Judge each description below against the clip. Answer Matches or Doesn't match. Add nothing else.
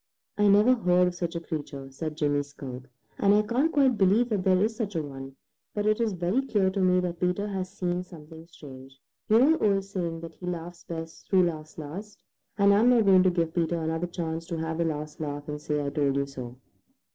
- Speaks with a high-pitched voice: Doesn't match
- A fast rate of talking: Matches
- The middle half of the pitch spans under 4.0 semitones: Doesn't match